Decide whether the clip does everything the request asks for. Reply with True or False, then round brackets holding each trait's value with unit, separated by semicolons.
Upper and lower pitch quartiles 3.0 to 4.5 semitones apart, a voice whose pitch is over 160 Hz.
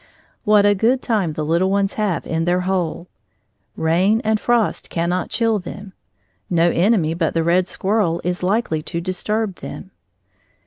True (3.7 semitones; 185 Hz)